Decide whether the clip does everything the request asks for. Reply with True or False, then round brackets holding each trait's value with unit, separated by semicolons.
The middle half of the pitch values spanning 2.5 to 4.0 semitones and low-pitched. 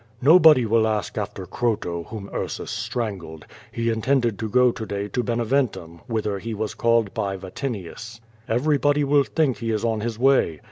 True (3.4 semitones; 115 Hz)